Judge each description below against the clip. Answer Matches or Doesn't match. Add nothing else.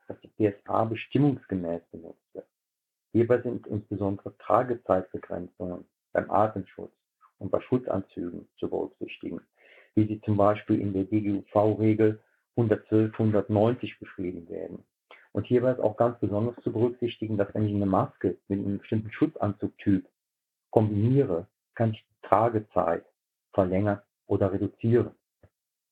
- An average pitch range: Doesn't match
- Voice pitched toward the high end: Doesn't match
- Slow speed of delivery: Matches